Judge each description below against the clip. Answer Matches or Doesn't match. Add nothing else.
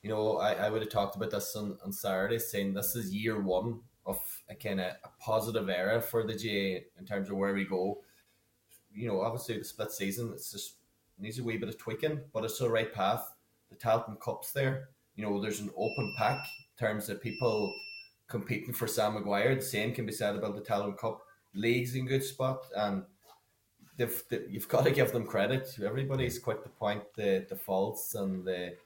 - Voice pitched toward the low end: Matches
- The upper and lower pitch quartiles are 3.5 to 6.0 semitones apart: Doesn't match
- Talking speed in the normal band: Doesn't match